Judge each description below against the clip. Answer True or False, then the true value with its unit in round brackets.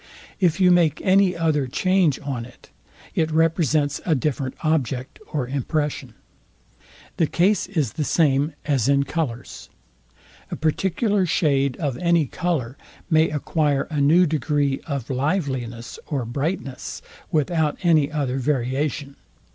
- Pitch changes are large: False (3.4 semitones)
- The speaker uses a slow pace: True (130 wpm)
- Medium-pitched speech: True (150 Hz)